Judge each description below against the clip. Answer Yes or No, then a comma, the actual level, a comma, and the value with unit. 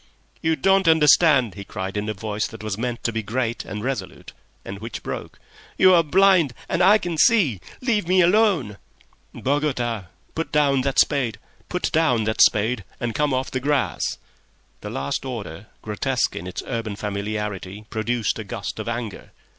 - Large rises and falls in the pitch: Yes, wide, 6.6 semitones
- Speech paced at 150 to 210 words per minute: Yes, average, 160 wpm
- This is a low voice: Yes, low, 120 Hz